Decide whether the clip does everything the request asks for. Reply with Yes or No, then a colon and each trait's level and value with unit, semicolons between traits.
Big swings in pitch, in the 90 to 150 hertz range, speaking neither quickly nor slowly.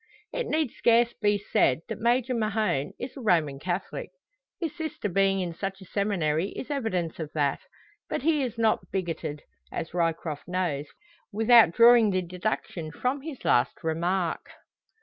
No: wide, 6.0 semitones; high, 195 Hz; average, 155 wpm